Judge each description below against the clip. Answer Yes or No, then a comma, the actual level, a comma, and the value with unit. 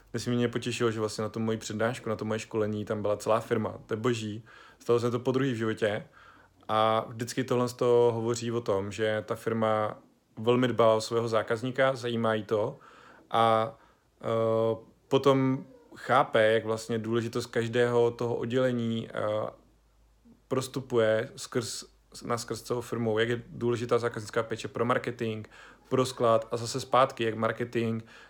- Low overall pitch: Yes, low, 115 Hz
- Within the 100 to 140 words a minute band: No, average, 165 wpm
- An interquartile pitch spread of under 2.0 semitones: Yes, narrow, 1.6 semitones